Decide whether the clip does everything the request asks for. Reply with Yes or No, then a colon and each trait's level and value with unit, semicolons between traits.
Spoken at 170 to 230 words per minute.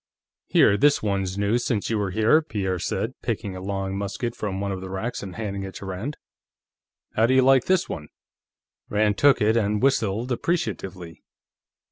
Yes: average, 180 wpm